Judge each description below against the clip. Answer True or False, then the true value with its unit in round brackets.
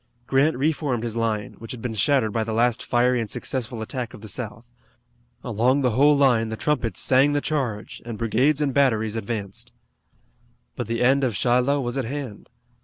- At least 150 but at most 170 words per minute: False (190 wpm)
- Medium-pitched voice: False (120 Hz)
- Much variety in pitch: False (3.4 semitones)